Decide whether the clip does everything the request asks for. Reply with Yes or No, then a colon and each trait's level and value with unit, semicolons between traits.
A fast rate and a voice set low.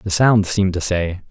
Yes: fast, 230 wpm; very low, 95 Hz